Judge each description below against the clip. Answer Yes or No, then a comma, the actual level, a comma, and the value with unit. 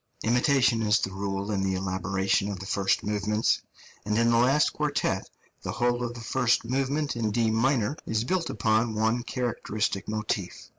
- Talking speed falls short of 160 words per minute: No, average, 170 wpm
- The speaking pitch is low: Yes, low, 110 Hz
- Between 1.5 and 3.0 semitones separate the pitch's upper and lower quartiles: No, average, 3.4 semitones